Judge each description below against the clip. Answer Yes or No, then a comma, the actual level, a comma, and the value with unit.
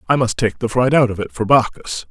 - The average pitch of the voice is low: Yes, low, 115 Hz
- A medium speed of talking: No, fast, 285 wpm